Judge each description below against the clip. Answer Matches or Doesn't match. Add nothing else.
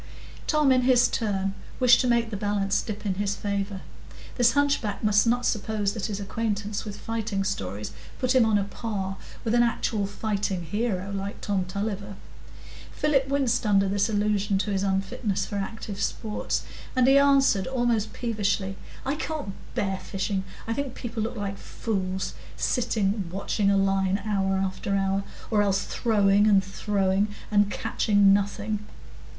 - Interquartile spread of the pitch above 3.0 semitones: Doesn't match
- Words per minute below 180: Matches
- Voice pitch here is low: Doesn't match